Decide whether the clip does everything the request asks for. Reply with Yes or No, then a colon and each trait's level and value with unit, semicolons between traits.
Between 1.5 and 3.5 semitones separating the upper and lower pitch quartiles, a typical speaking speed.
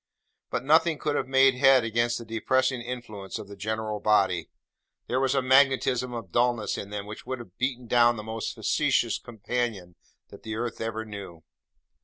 Yes: average, 3.2 semitones; average, 180 wpm